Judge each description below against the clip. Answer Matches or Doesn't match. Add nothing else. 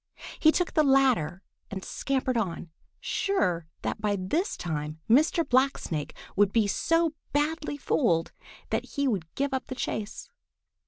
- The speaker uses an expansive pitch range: Matches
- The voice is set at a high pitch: Matches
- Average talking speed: Matches